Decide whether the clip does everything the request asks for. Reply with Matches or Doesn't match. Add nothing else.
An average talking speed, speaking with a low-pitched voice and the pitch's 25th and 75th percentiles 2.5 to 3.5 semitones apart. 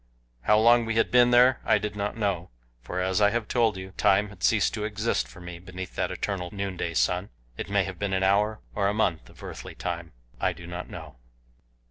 Doesn't match